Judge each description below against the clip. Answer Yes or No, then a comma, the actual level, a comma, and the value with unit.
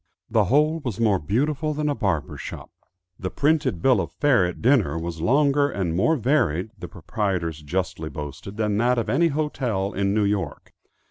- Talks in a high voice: No, low, 105 Hz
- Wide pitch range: Yes, wide, 7.3 semitones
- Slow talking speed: No, average, 180 wpm